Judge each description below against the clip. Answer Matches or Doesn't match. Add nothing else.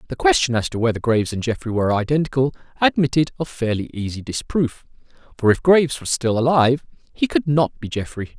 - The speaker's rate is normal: Matches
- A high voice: Doesn't match